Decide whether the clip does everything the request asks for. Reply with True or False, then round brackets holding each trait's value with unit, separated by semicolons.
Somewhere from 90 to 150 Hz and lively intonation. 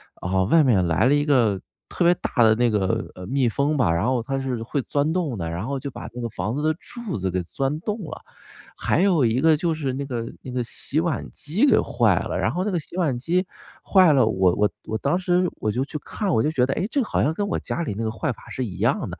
True (135 Hz; 6.5 semitones)